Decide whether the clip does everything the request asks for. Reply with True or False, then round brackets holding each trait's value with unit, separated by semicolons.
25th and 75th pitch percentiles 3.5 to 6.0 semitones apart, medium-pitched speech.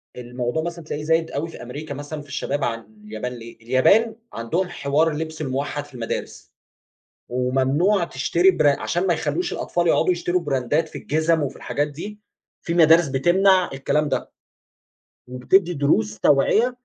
True (4.4 semitones; 150 Hz)